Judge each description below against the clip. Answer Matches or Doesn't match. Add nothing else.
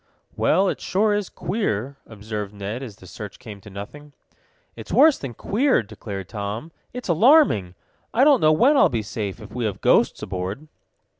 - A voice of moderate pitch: Doesn't match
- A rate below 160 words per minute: Doesn't match